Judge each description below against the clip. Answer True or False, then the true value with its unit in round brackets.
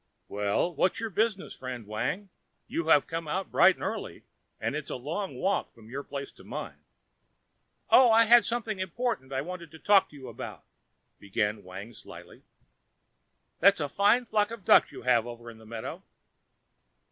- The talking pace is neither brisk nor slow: True (175 wpm)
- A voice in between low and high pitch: True (160 Hz)